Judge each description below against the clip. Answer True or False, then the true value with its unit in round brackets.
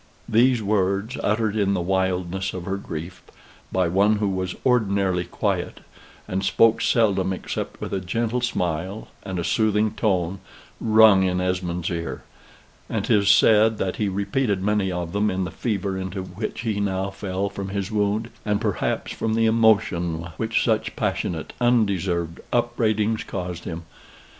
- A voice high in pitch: False (100 Hz)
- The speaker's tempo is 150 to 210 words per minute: True (155 wpm)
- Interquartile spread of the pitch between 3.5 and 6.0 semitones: False (2.9 semitones)